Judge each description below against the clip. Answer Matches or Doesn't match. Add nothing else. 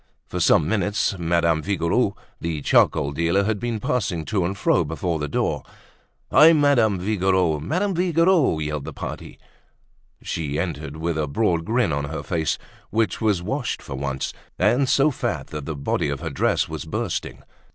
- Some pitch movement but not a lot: Doesn't match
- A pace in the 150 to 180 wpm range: Matches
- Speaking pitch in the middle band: Doesn't match